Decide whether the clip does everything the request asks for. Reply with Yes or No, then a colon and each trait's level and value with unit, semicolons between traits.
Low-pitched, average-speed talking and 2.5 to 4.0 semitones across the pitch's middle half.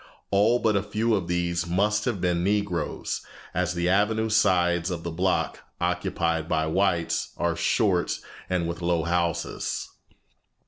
Yes: very low, 90 Hz; average, 145 wpm; average, 2.8 semitones